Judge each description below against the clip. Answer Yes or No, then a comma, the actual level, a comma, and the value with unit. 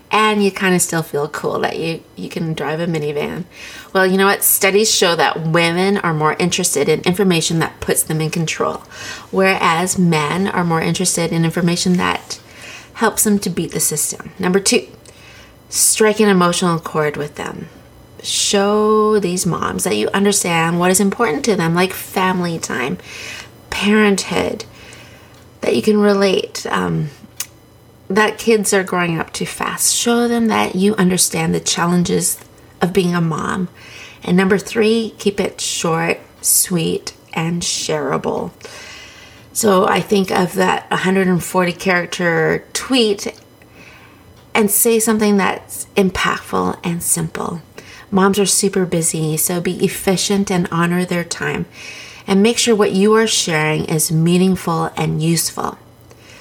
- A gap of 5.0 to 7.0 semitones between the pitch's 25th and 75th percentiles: No, average, 3.5 semitones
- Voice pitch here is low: No, medium, 185 Hz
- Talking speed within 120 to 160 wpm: Yes, average, 145 wpm